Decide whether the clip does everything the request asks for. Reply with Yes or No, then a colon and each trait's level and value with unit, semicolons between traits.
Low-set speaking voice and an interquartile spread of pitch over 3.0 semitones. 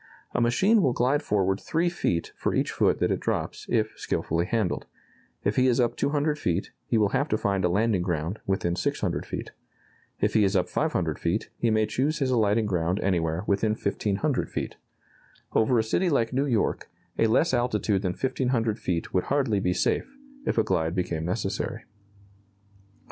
Yes: low, 110 Hz; average, 5.3 semitones